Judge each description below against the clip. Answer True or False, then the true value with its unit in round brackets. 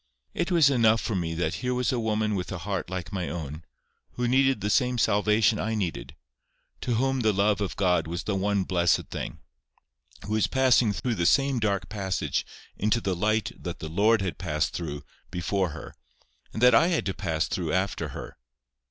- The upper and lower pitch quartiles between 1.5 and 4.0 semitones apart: False (4.4 semitones)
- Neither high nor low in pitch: False (100 Hz)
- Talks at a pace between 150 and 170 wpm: False (195 wpm)